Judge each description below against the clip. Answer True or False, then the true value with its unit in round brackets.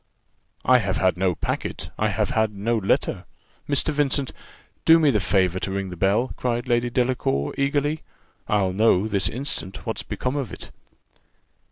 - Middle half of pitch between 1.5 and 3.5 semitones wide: False (5.5 semitones)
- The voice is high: False (110 Hz)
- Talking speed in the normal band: True (165 wpm)